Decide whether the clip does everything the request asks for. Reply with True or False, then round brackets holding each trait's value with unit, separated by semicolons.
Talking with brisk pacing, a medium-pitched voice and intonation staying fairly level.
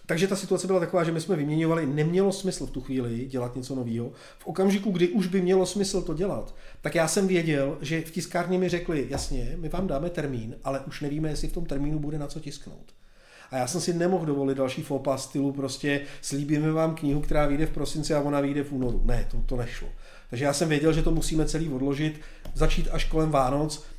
False (225 wpm; 155 Hz; 3.9 semitones)